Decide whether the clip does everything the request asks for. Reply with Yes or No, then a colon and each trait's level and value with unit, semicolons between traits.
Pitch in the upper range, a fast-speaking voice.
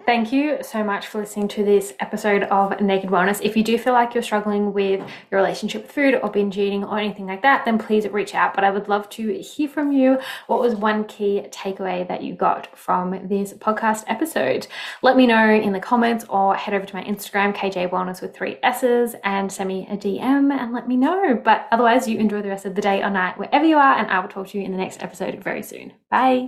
Yes: high, 210 Hz; fast, 245 wpm